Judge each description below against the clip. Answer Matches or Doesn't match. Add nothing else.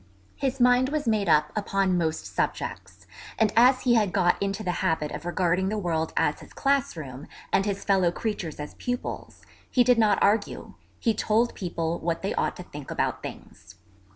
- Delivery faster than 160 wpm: Matches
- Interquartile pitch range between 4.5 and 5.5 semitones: Matches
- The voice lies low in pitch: Doesn't match